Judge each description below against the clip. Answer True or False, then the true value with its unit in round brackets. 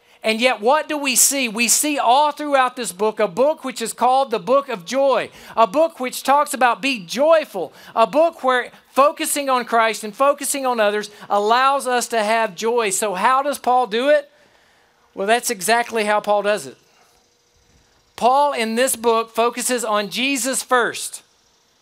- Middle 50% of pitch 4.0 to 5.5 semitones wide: False (3.4 semitones)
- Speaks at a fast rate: False (175 wpm)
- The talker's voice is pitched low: False (245 Hz)